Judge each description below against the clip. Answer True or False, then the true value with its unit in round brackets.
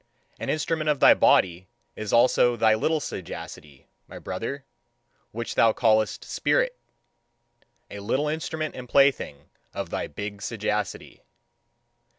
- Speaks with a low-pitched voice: True (115 Hz)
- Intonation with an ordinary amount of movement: False (6.0 semitones)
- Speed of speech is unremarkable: False (125 wpm)